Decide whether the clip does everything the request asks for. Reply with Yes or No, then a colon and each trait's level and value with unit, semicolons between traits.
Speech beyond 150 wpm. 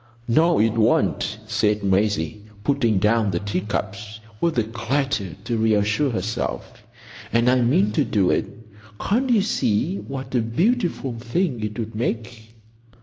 No: average, 145 wpm